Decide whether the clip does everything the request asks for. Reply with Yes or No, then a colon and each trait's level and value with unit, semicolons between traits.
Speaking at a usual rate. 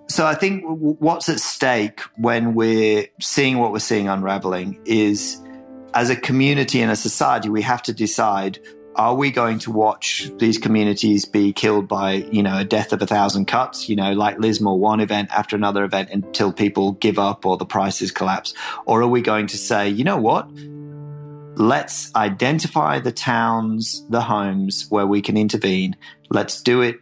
Yes: average, 180 wpm